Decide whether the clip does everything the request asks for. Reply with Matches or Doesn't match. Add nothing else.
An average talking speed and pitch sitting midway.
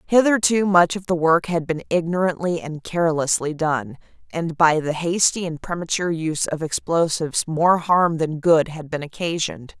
Matches